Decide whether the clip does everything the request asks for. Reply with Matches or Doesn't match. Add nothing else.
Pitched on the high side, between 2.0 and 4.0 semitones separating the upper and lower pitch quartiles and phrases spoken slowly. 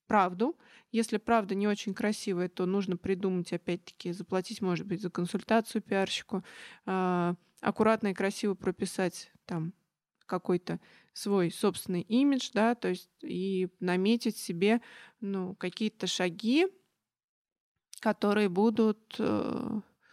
Matches